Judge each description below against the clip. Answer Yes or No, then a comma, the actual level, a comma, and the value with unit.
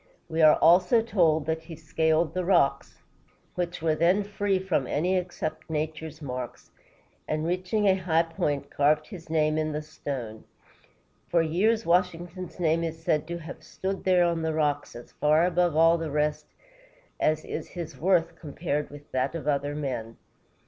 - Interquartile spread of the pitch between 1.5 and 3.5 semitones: Yes, average, 2.7 semitones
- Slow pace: No, average, 170 wpm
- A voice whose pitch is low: No, medium, 160 Hz